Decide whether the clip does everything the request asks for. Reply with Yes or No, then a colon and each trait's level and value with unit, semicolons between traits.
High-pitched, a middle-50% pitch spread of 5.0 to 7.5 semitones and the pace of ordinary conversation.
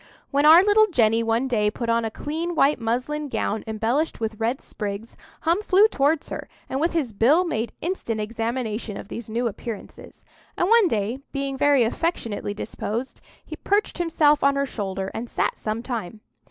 Yes: high, 245 Hz; wide, 5.4 semitones; average, 175 wpm